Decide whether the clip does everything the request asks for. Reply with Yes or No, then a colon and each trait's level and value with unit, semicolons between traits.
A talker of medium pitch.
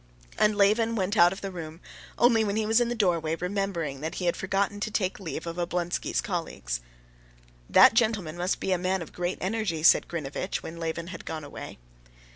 Yes: medium, 180 Hz